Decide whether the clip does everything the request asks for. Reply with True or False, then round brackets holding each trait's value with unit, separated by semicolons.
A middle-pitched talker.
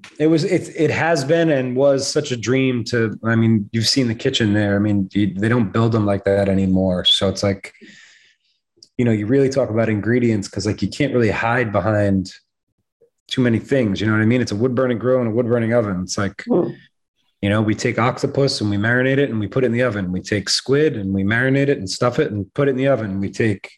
False (115 Hz)